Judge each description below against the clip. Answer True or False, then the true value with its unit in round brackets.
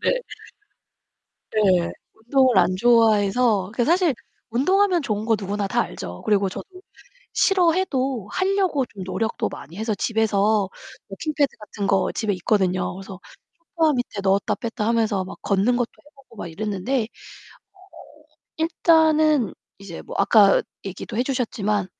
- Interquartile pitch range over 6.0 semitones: False (5.4 semitones)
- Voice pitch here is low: False (220 Hz)